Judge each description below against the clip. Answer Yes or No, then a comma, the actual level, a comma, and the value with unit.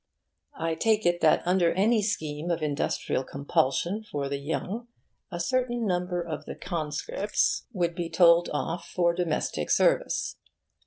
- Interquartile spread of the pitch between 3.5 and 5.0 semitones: Yes, average, 4.1 semitones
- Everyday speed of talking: Yes, average, 145 wpm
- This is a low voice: No, medium, 175 Hz